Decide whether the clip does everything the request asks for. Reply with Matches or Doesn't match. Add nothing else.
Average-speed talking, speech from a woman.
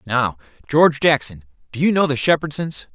Doesn't match